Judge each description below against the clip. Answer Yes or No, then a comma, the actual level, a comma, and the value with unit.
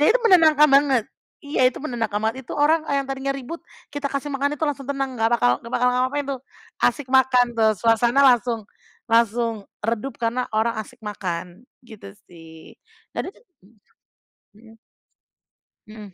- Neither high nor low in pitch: No, very high, 250 Hz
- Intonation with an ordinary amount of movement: Yes, average, 3.7 semitones